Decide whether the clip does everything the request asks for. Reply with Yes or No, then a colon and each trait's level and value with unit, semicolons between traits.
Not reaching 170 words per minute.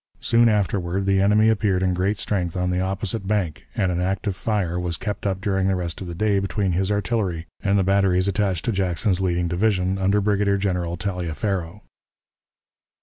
No: average, 185 wpm